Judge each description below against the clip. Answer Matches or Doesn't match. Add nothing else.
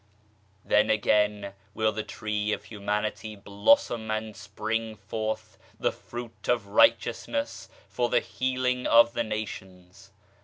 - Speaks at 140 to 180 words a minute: Matches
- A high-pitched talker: Doesn't match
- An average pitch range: Doesn't match